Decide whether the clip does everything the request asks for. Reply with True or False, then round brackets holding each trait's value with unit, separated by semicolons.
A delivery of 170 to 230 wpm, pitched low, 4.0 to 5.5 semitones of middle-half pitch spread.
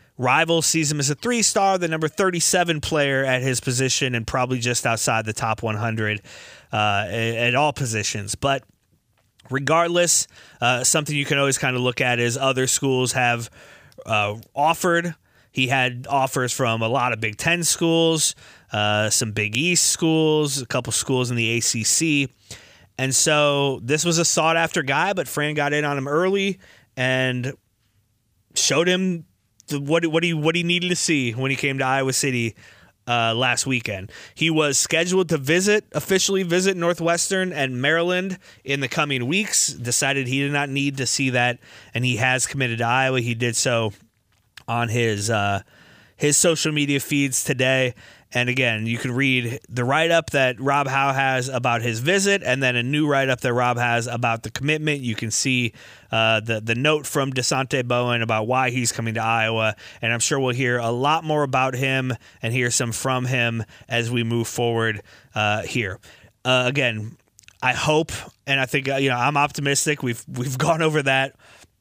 True (180 wpm; 130 Hz; 4.3 semitones)